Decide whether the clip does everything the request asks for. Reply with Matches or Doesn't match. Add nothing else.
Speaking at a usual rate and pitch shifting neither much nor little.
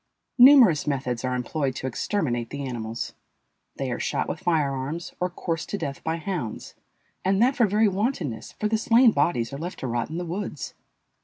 Doesn't match